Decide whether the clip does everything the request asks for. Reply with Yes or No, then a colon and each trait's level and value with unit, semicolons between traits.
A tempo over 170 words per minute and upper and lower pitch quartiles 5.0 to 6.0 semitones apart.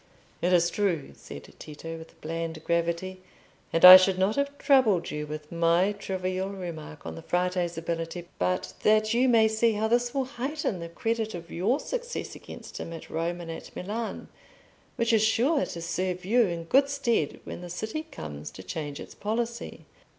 Yes: average, 180 wpm; wide, 5.4 semitones